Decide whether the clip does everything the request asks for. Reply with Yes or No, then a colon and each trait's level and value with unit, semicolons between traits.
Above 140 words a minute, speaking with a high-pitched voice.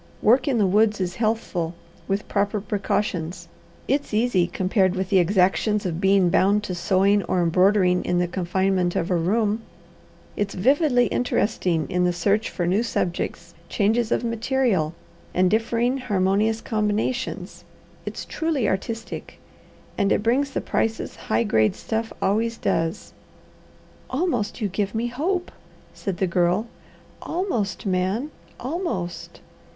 No: slow, 135 wpm; high, 205 Hz